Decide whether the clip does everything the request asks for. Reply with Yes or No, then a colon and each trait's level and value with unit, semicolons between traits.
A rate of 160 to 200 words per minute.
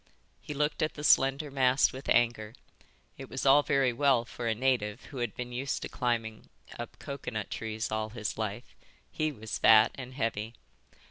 Yes: average, 180 wpm